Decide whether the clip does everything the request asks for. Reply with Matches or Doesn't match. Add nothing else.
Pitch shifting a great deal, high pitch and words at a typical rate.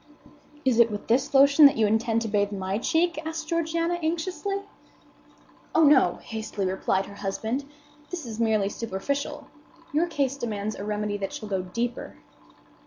Matches